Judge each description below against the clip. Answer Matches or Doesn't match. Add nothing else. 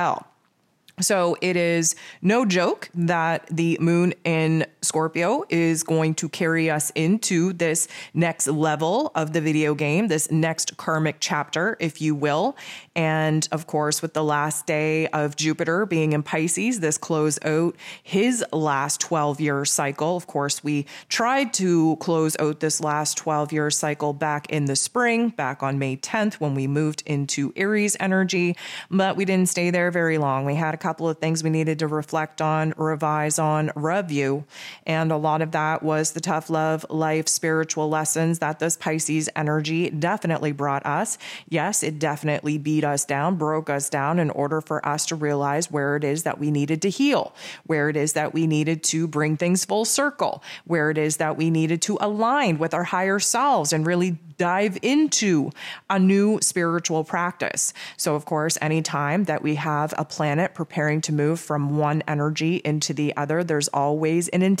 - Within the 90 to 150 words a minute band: Doesn't match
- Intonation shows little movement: Matches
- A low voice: Doesn't match